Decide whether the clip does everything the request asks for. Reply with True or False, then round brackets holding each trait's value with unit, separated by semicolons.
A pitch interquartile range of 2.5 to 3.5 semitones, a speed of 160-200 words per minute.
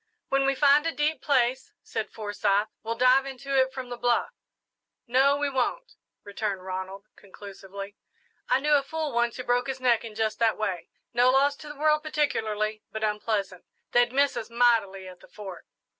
False (4.5 semitones; 185 wpm)